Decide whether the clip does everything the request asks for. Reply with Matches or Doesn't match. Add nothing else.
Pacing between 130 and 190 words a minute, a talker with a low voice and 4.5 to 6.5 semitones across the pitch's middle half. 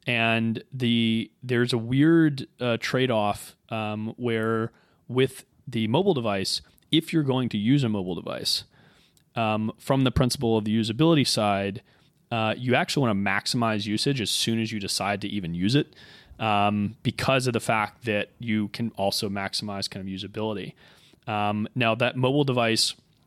Doesn't match